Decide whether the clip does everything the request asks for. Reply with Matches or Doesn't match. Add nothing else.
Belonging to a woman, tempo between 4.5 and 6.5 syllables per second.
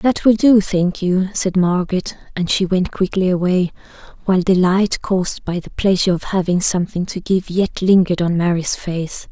Matches